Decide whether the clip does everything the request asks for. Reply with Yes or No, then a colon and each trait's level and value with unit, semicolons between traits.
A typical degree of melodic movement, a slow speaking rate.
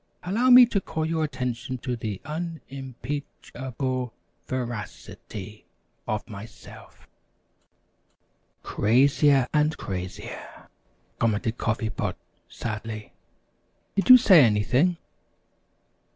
No: wide, 5.7 semitones; slow, 110 wpm